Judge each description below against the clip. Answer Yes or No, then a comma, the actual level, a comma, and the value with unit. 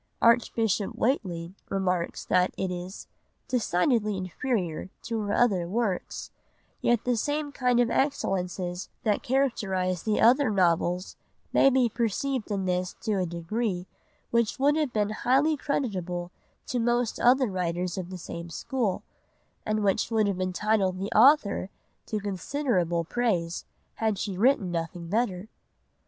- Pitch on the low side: No, high, 205 Hz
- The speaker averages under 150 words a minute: Yes, slow, 135 wpm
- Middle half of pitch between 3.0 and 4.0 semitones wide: No, average, 5.0 semitones